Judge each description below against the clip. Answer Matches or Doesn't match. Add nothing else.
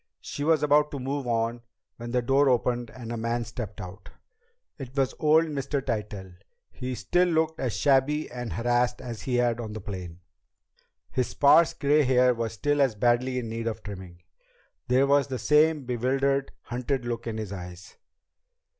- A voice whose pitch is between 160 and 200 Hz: Doesn't match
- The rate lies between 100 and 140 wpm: Doesn't match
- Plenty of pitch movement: Doesn't match